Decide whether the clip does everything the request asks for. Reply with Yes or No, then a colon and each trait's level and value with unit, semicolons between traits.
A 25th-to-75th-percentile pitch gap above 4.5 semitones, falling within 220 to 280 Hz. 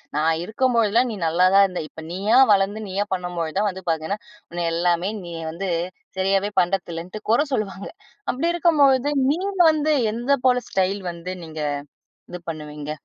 No: average, 4.9 semitones; high, 190 Hz